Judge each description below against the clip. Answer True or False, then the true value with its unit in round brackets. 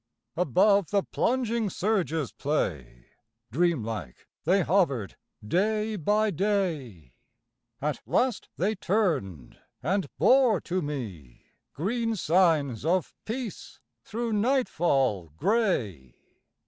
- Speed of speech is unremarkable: False (95 wpm)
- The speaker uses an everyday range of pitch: False (8.5 semitones)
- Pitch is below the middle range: False (175 Hz)